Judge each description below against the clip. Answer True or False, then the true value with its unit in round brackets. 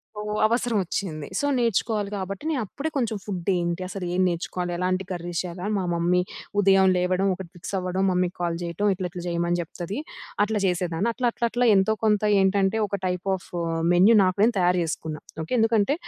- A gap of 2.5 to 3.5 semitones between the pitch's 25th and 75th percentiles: True (2.9 semitones)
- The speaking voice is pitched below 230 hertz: True (185 Hz)